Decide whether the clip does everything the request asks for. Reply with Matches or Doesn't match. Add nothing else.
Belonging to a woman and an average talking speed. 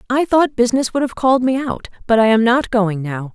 Doesn't match